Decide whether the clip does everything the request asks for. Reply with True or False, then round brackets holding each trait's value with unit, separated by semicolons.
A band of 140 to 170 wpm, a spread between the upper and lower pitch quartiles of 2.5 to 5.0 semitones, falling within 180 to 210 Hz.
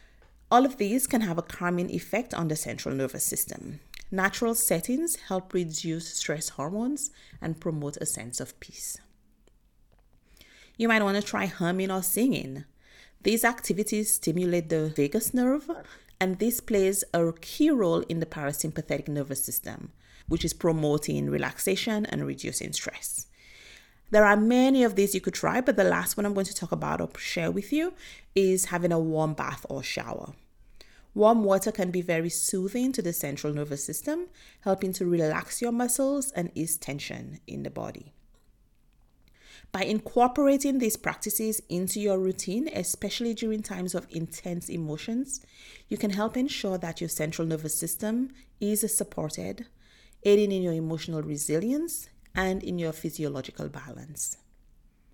False (155 wpm; 5.4 semitones; 190 Hz)